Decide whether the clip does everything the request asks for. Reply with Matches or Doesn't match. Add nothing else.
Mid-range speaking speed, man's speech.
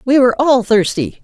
Doesn't match